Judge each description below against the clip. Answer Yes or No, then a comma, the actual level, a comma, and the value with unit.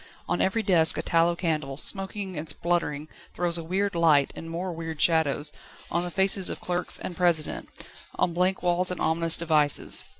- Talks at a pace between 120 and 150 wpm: No, average, 175 wpm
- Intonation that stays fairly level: Yes, narrow, 2.1 semitones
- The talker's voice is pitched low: No, medium, 170 Hz